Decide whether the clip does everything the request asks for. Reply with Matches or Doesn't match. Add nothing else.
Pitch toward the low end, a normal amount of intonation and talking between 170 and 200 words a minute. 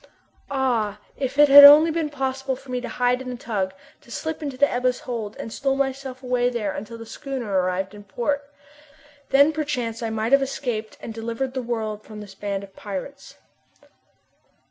Doesn't match